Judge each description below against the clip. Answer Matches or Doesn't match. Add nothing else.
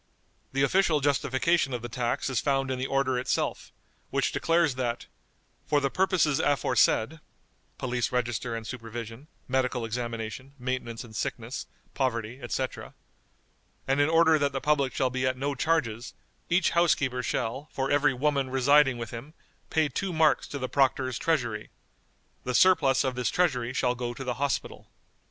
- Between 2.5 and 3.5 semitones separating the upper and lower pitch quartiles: Matches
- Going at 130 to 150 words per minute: Doesn't match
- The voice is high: Doesn't match